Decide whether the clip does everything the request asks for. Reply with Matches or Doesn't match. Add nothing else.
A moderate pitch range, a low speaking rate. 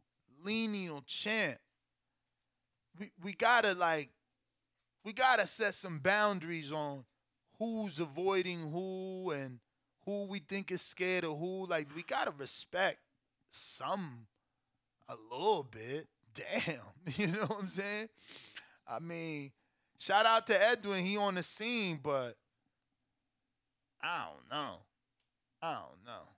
Doesn't match